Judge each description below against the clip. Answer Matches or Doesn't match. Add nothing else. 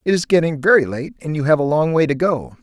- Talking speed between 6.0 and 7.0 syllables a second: Matches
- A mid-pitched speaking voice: Matches